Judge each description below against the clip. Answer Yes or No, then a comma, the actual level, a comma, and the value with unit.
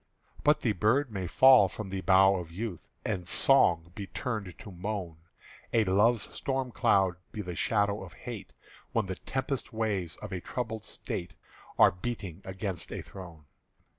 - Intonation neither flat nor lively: Yes, average, 3.9 semitones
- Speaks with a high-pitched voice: No, low, 100 Hz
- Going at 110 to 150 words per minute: No, average, 165 wpm